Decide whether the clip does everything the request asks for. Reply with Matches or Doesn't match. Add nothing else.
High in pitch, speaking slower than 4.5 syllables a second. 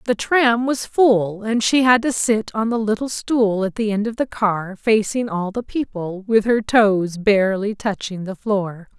Matches